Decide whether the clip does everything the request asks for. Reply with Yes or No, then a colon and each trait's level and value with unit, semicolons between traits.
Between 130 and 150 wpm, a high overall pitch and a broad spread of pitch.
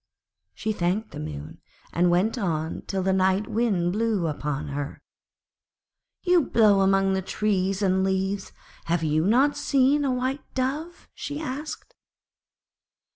Yes: average, 140 wpm; high, 195 Hz; wide, 6.3 semitones